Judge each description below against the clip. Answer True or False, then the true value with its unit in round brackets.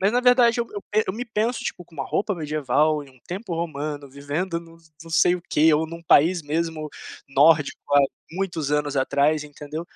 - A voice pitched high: False (160 Hz)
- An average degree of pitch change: True (3.8 semitones)